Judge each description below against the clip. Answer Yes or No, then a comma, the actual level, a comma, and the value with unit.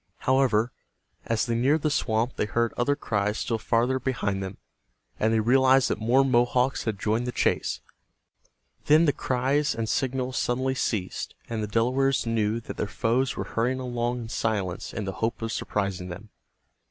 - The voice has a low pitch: Yes, low, 120 Hz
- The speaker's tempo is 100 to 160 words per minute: No, average, 175 wpm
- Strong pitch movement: No, average, 3.0 semitones